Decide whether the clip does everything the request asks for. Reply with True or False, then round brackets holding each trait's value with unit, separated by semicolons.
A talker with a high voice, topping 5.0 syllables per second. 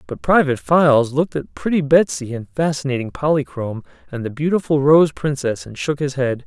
False (140 Hz; 5.6 syllables/s)